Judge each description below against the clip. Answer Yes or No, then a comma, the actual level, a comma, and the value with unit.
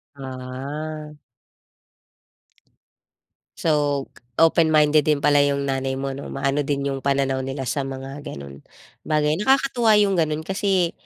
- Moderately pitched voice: Yes, medium, 145 Hz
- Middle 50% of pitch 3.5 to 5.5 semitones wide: No, narrow, 2.5 semitones